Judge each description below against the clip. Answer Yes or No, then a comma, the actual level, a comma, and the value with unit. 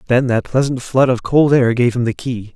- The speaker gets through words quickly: Yes, fast, 260 wpm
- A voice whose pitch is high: No, low, 125 Hz